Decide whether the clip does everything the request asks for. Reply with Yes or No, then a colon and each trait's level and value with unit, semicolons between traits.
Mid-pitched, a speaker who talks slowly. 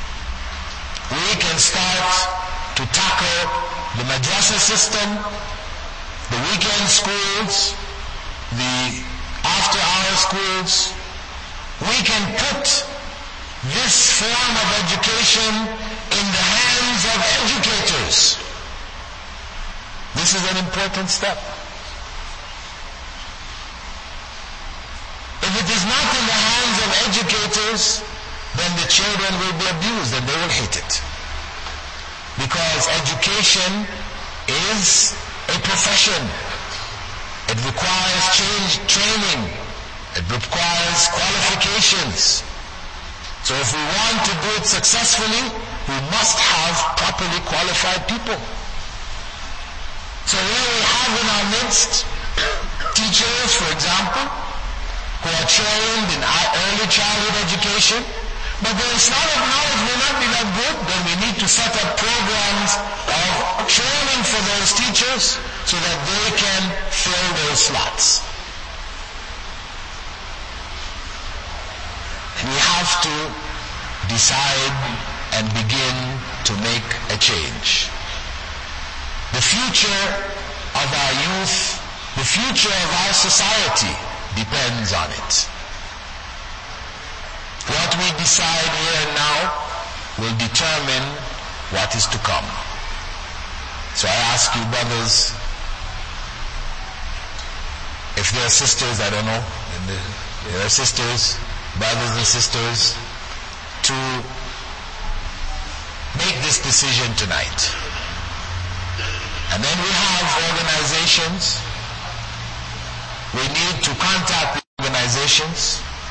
No: low, 125 Hz; slow, 100 wpm